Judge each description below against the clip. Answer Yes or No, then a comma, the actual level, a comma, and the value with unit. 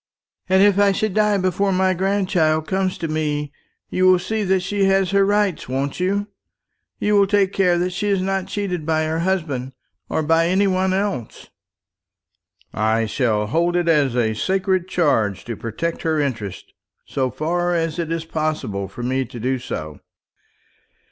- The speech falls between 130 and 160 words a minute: No, average, 170 wpm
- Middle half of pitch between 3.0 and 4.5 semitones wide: No, average, 5.2 semitones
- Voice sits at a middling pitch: Yes, medium, 175 Hz